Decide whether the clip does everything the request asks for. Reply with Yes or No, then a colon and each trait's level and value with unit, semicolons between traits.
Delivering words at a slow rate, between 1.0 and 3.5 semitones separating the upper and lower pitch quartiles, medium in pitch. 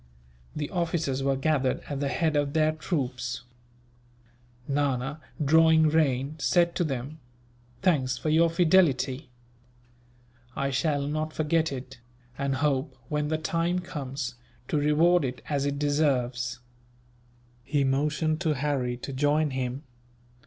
Yes: slow, 130 wpm; average, 2.8 semitones; medium, 145 Hz